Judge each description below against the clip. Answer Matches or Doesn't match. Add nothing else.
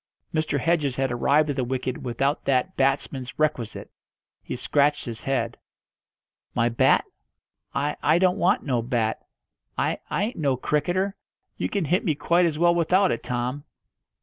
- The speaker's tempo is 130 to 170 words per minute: Matches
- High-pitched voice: Doesn't match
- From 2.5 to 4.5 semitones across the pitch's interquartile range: Doesn't match